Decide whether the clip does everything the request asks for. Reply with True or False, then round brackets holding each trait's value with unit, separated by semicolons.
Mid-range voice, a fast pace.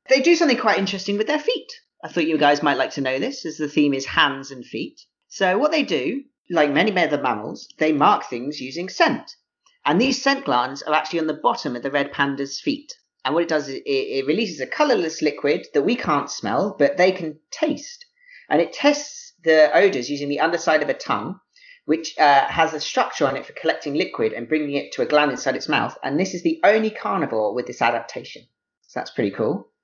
True (180 Hz; 225 wpm)